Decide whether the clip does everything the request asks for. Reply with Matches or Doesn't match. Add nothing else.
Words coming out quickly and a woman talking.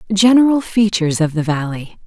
Doesn't match